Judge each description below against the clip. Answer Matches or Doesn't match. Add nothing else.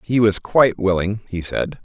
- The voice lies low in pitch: Matches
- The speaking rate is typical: Matches